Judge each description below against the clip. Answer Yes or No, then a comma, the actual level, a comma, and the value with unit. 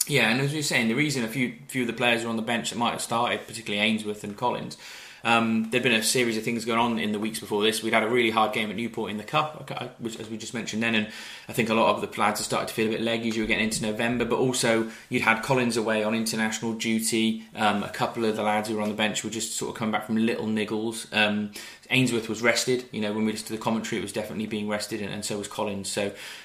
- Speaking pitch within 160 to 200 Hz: No, low, 110 Hz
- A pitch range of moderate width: No, narrow, 1.3 semitones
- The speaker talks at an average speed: No, fast, 295 wpm